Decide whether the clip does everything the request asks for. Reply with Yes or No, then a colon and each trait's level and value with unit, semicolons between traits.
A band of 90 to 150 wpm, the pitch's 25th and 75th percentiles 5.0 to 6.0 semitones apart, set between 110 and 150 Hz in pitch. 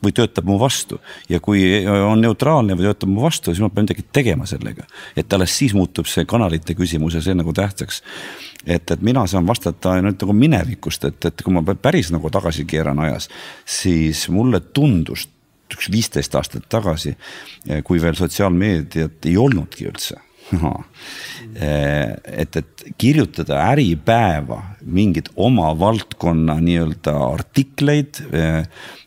No: average, 140 wpm; average, 5.3 semitones; very low, 95 Hz